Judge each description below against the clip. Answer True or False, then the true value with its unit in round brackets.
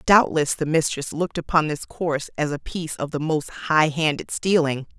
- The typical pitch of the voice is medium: True (155 Hz)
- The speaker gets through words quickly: False (180 wpm)